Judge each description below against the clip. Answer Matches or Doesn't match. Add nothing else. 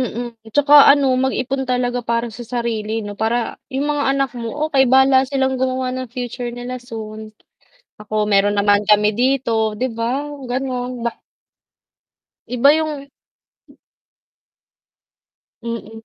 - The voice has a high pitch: Matches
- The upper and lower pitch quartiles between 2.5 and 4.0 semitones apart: Matches